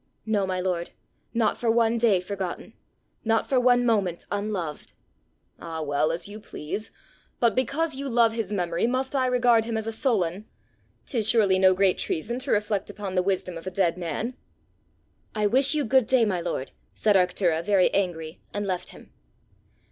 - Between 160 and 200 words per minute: Yes, average, 180 wpm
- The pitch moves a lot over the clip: No, average, 4.4 semitones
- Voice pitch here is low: No, high, 205 Hz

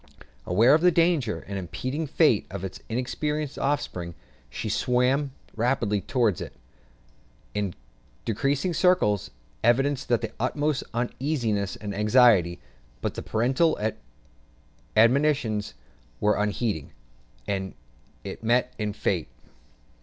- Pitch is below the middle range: Yes, low, 120 Hz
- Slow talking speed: Yes, slow, 110 wpm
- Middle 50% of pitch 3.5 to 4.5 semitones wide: No, average, 5.3 semitones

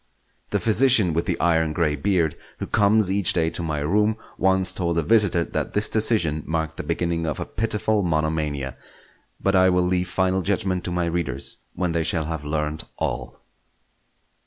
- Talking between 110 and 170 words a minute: No, average, 180 wpm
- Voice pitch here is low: Yes, very low, 85 Hz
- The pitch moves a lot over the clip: No, average, 3.5 semitones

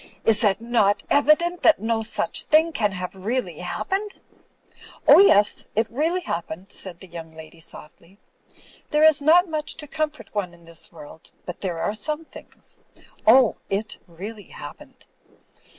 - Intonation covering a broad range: Yes, wide, 8.8 semitones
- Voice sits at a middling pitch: No, high, 220 Hz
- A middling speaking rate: Yes, average, 165 wpm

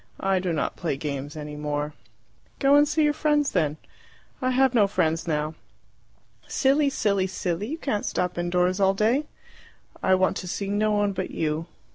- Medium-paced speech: Yes, average, 175 wpm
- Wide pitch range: Yes, wide, 7.9 semitones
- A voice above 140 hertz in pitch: Yes, high, 190 Hz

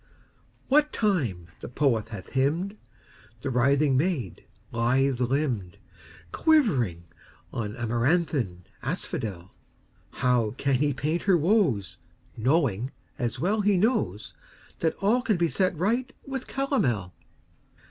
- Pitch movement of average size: No, wide, 8.3 semitones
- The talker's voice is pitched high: No, low, 135 Hz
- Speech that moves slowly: Yes, slow, 115 wpm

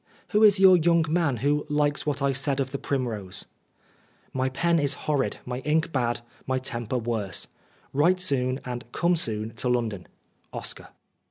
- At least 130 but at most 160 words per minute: No, average, 180 wpm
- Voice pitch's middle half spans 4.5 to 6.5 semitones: No, average, 4.0 semitones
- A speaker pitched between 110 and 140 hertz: Yes, low, 135 Hz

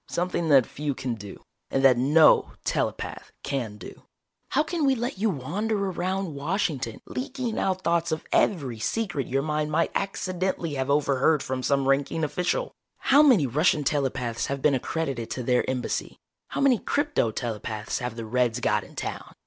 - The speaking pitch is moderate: Yes, medium, 150 Hz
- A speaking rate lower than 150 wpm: No, average, 170 wpm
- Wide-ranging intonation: Yes, wide, 6.6 semitones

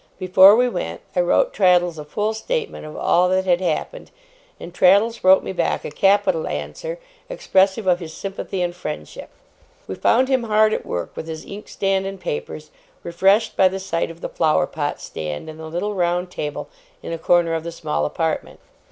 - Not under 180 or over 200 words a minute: Yes, average, 190 wpm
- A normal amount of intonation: Yes, average, 3.8 semitones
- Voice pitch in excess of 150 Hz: Yes, medium, 185 Hz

